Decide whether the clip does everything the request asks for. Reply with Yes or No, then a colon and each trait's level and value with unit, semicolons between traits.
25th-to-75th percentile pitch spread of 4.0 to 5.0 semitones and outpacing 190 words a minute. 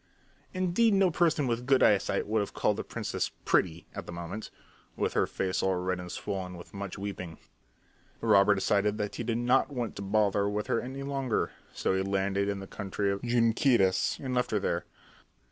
Yes: average, 4.3 semitones; average, 200 wpm